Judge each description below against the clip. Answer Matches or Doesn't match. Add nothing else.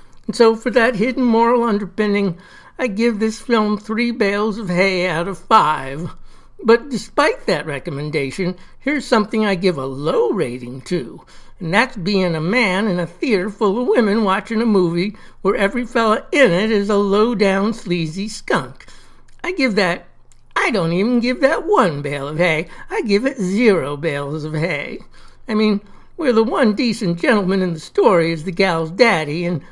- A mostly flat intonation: Doesn't match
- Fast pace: Doesn't match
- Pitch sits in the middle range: Doesn't match